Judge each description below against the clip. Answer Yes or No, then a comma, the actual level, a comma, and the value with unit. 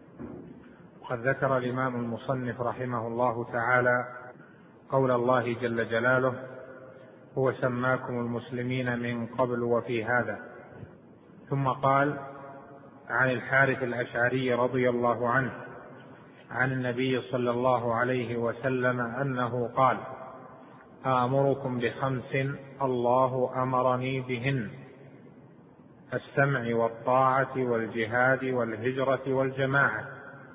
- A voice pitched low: Yes, low, 125 Hz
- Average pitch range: No, narrow, 1.5 semitones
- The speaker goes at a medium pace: Yes, average, 85 wpm